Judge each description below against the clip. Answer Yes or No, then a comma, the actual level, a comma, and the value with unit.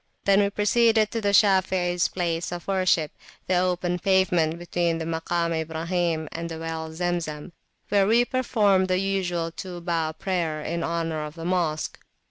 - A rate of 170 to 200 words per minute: No, average, 150 wpm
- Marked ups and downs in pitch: No, narrow, 2.5 semitones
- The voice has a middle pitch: Yes, medium, 175 Hz